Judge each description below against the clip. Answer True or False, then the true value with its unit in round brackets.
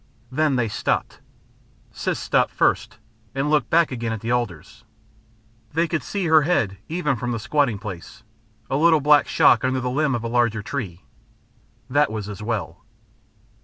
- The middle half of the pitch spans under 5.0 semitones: False (5.6 semitones)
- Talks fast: False (165 wpm)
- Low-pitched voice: True (125 Hz)